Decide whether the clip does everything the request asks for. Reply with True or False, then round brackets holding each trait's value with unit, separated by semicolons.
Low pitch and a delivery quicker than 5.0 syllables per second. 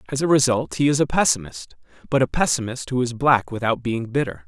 True (125 Hz; 5.8 syllables/s)